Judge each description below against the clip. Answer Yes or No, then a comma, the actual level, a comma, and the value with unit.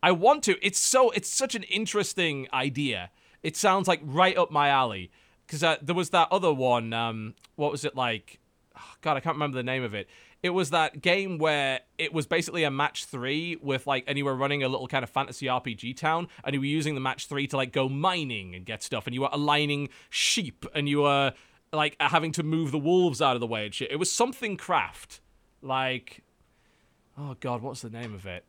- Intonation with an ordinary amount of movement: Yes, average, 4.2 semitones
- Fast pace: Yes, fast, 230 wpm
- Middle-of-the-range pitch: Yes, medium, 145 Hz